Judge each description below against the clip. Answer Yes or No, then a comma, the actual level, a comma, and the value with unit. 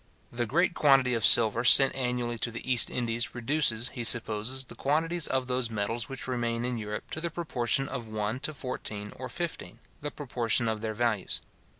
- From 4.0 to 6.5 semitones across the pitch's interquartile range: No, average, 2.8 semitones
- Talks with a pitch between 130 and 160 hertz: No, low, 120 Hz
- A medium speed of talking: Yes, average, 190 wpm